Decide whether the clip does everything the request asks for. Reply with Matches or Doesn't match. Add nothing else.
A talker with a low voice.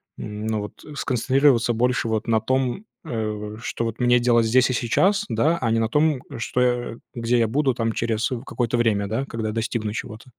Matches